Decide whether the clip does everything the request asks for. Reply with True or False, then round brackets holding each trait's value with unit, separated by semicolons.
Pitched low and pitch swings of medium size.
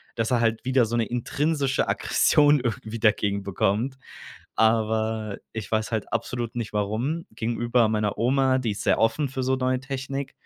True (115 Hz; 3.0 semitones)